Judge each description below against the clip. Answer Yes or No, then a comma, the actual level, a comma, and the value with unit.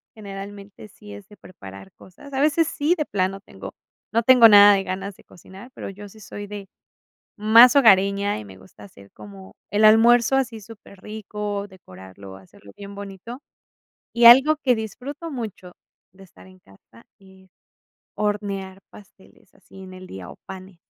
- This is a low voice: No, high, 200 Hz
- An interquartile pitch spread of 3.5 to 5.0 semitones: No, average, 3.1 semitones